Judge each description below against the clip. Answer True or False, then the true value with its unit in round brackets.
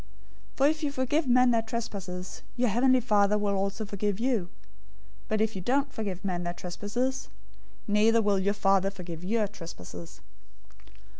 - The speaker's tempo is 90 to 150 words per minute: False (170 wpm)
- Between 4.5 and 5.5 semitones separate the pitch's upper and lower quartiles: False (4.0 semitones)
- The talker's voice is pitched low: False (210 Hz)